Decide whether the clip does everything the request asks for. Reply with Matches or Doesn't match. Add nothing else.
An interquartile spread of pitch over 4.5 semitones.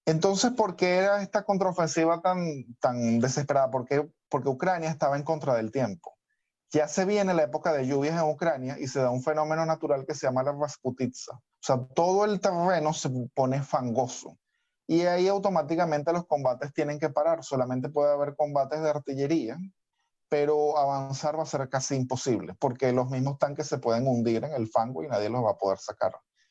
Doesn't match